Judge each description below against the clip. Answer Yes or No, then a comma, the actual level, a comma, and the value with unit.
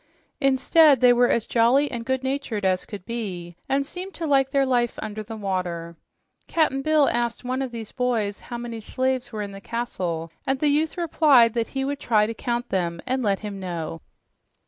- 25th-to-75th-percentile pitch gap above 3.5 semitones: Yes, average, 4.7 semitones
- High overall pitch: Yes, high, 240 Hz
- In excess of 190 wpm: Yes, average, 200 wpm